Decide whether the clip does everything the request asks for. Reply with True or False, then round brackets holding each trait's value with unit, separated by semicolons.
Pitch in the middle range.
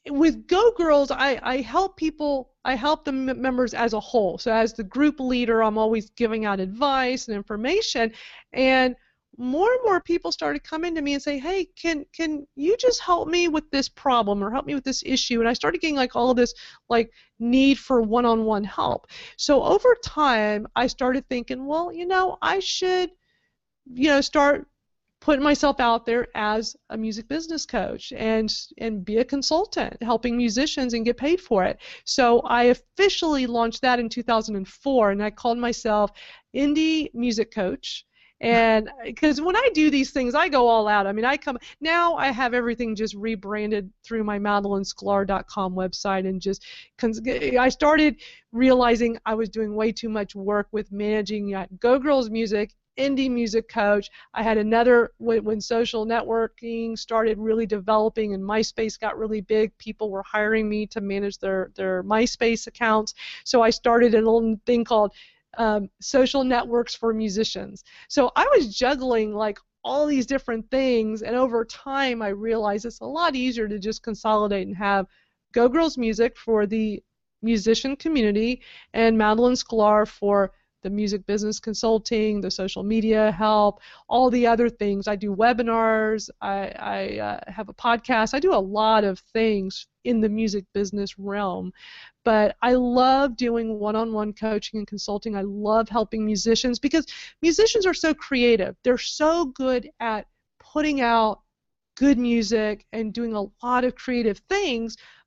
False (230 Hz)